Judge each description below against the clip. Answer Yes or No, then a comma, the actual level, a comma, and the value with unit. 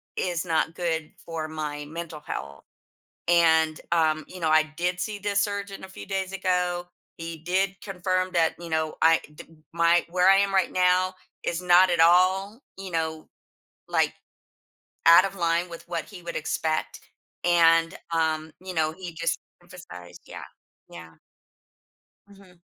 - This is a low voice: No, medium, 170 Hz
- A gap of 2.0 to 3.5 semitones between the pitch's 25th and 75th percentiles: Yes, narrow, 2.4 semitones